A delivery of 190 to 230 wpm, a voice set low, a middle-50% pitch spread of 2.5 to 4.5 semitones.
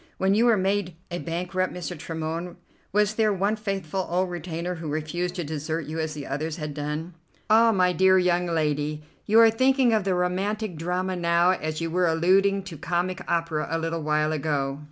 No: average, 195 wpm; medium, 175 Hz; average, 3.1 semitones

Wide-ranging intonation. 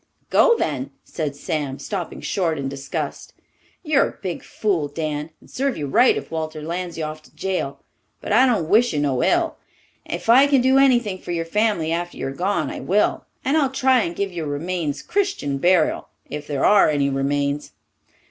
Yes: wide, 7.2 semitones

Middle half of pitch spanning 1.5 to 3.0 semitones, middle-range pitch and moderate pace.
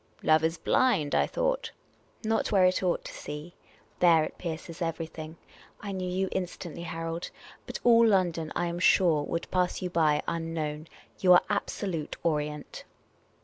Yes: narrow, 2.6 semitones; medium, 170 Hz; average, 165 wpm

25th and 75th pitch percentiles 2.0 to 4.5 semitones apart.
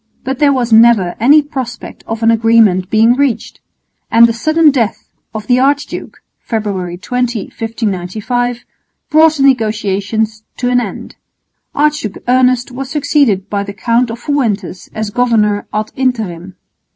Yes: average, 3.3 semitones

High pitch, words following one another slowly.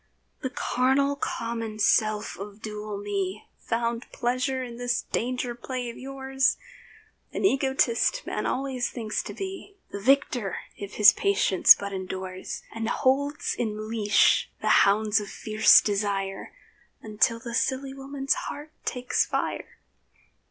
Yes: high, 235 Hz; slow, 130 wpm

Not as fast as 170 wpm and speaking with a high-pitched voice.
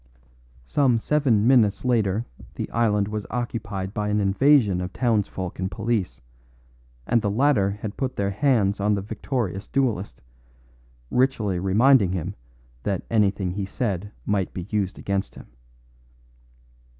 No: slow, 135 wpm; low, 105 Hz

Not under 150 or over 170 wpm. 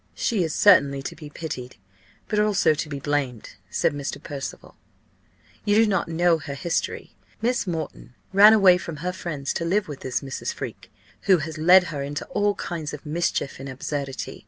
No: average, 180 wpm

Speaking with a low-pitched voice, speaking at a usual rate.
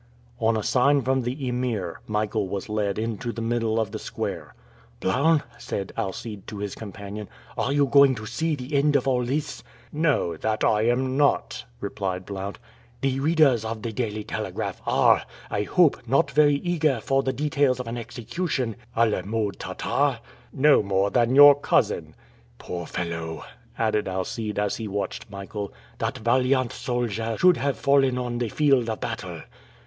Yes: low, 120 Hz; average, 170 wpm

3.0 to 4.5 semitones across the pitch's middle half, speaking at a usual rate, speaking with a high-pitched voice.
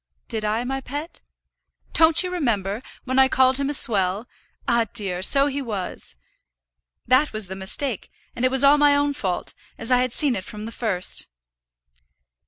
No: average, 4.9 semitones; average, 180 wpm; very high, 250 Hz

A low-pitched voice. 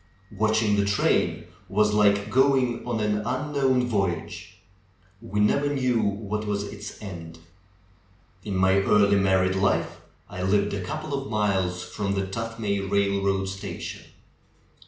Yes: low, 100 Hz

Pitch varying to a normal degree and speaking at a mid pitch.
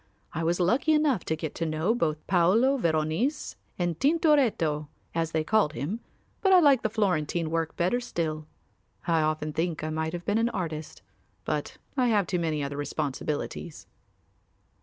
No: wide, 6.4 semitones; medium, 170 Hz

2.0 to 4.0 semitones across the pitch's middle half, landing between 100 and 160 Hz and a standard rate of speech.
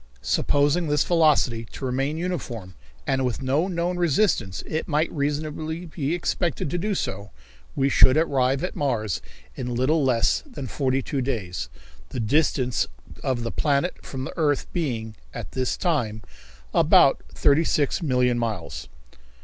No: average, 4.5 semitones; medium, 140 Hz; average, 150 wpm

